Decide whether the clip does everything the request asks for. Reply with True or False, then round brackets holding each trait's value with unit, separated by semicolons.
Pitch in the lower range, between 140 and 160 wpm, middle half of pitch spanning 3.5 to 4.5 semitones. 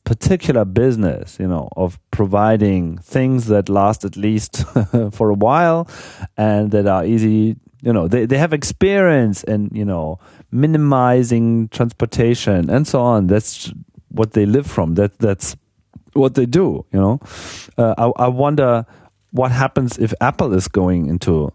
True (110 Hz; 155 wpm; 4.1 semitones)